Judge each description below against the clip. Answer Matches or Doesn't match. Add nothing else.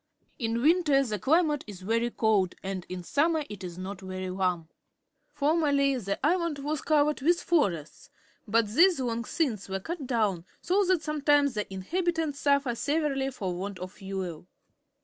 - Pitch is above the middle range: Matches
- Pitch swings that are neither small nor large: Doesn't match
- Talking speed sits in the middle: Matches